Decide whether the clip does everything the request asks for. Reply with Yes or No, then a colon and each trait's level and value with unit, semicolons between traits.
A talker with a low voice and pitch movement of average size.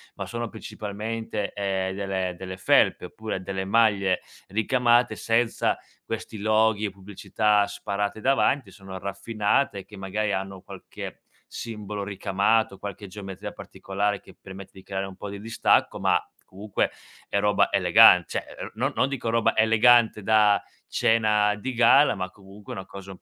No: low, 105 Hz; narrow, 2.3 semitones